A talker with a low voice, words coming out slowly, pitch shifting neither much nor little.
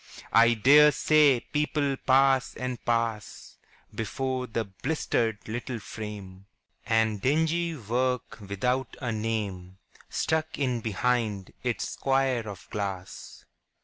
Yes: low, 120 Hz; slow, 110 wpm; average, 3.9 semitones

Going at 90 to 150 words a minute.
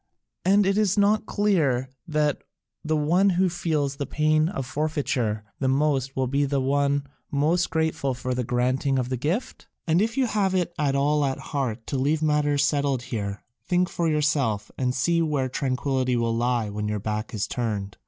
No: average, 185 wpm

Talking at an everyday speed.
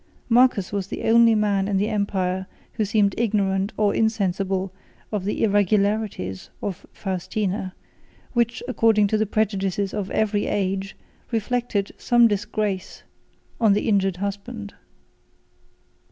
No: slow, 125 wpm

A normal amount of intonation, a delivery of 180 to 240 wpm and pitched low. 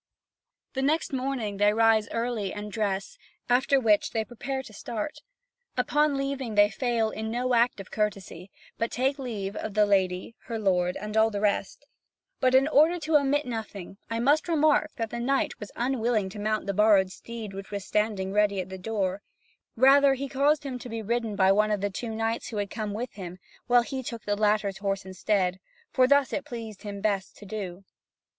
No: average, 4.0 semitones; average, 200 wpm; high, 220 Hz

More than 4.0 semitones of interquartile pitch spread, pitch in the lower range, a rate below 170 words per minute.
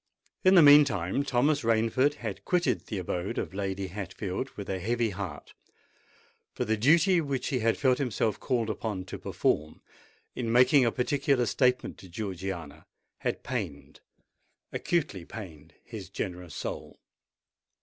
Yes: wide, 5.5 semitones; low, 110 Hz; average, 140 wpm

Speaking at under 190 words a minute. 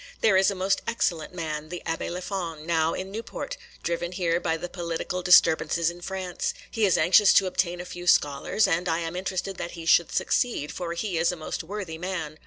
No: fast, 205 wpm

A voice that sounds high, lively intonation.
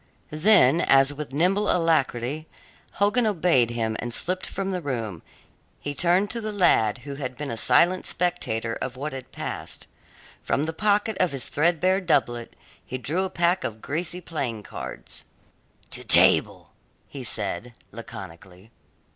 No: medium, 150 Hz; wide, 6.9 semitones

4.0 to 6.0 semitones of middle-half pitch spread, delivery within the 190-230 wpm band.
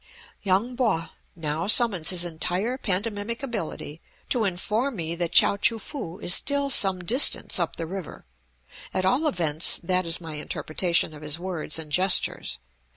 No: average, 5.1 semitones; average, 155 wpm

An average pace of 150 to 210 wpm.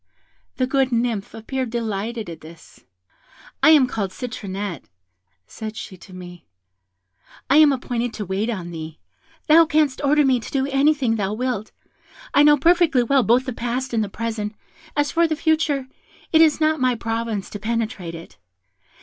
Yes: average, 165 wpm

